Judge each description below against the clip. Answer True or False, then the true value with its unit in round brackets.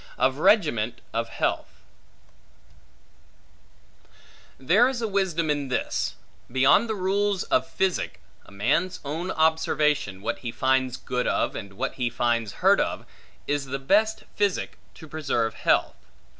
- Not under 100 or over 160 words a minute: True (135 wpm)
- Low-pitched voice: False (145 Hz)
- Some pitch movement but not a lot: False (7.4 semitones)